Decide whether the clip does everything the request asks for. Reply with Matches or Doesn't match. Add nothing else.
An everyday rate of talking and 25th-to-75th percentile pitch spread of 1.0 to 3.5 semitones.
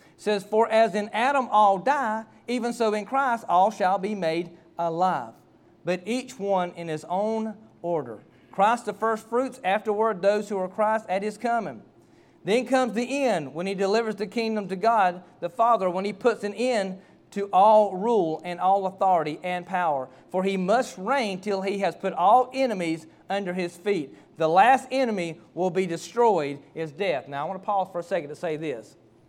Doesn't match